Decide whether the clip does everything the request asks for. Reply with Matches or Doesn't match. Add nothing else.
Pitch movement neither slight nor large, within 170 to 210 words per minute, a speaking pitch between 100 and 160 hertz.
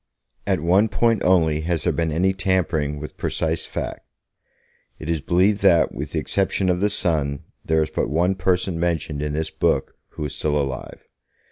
Doesn't match